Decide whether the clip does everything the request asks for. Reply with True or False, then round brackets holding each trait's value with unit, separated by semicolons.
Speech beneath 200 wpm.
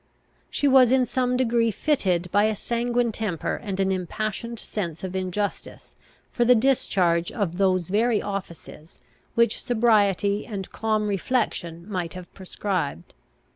True (135 wpm)